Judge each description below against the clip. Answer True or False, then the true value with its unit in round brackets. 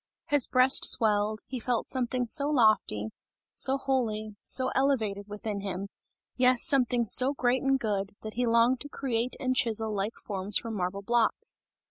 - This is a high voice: True (235 Hz)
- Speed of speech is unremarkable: True (160 wpm)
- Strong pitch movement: False (3.6 semitones)